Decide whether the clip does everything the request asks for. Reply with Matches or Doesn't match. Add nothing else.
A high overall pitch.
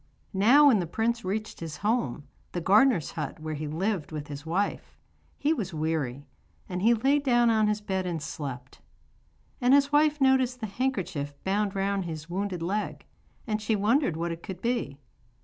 Matches